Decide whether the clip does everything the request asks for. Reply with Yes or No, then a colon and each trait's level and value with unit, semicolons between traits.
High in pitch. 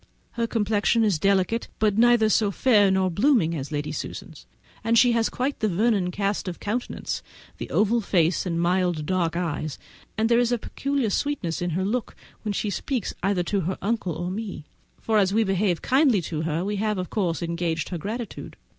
Yes: high, 200 Hz